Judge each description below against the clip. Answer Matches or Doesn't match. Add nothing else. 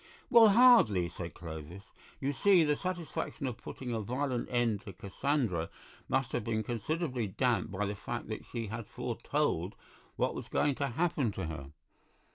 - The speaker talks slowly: Doesn't match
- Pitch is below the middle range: Matches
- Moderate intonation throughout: Doesn't match